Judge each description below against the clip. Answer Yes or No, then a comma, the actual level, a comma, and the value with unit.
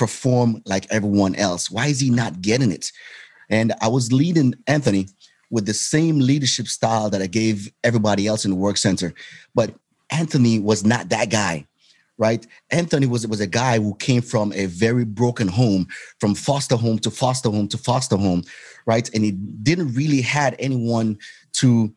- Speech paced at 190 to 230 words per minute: No, average, 180 wpm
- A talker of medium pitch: No, low, 115 Hz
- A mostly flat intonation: No, average, 3.5 semitones